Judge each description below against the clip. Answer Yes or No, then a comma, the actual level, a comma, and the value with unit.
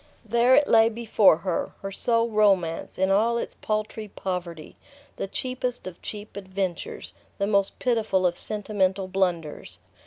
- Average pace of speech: Yes, average, 145 wpm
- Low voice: No, high, 200 Hz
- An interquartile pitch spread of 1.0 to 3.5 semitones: Yes, average, 3.0 semitones